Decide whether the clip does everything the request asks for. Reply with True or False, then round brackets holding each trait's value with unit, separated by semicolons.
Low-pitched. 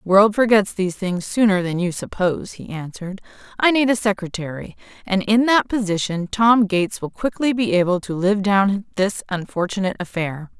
False (195 Hz)